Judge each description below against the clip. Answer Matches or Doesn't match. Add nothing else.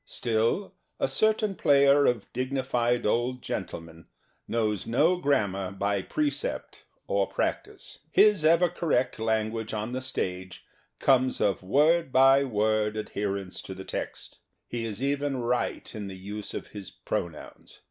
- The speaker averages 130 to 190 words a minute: Matches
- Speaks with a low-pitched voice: Matches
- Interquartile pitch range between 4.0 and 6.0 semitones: Matches